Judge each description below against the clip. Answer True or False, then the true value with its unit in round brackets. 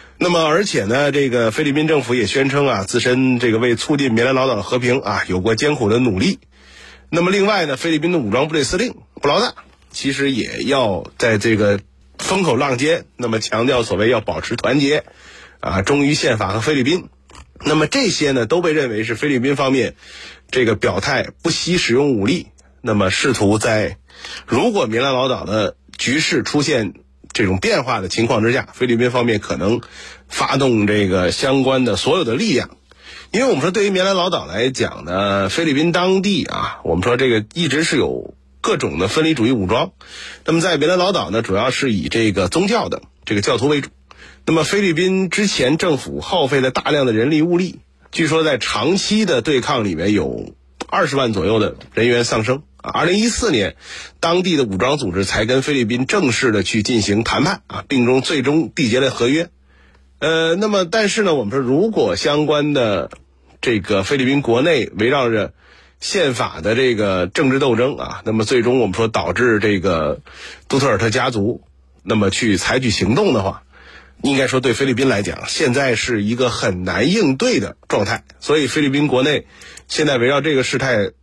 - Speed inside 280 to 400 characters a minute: True (285 characters per minute)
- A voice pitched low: True (125 Hz)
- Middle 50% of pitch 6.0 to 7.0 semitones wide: True (6.5 semitones)